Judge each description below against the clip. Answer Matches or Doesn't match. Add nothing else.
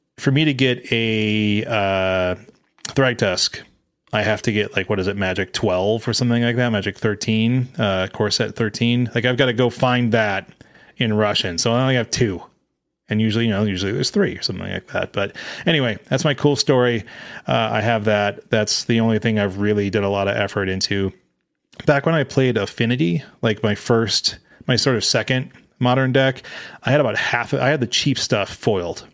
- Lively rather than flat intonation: Doesn't match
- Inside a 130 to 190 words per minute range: Doesn't match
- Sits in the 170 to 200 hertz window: Doesn't match